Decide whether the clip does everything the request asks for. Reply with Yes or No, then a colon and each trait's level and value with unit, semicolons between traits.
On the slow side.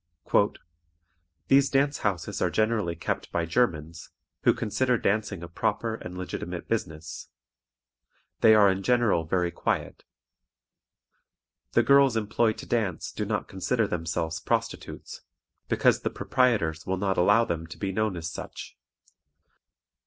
Yes: slow, 130 wpm